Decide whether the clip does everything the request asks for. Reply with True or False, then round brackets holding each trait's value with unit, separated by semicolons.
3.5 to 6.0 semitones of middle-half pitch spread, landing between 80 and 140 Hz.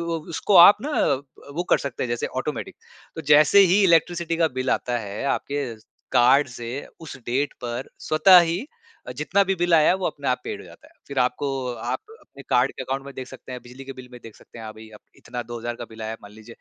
True (5.2 semitones; 135 Hz)